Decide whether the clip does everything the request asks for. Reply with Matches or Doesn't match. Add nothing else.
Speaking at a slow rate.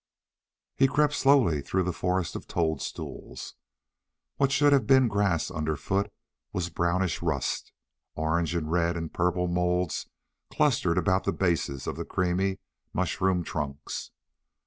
Matches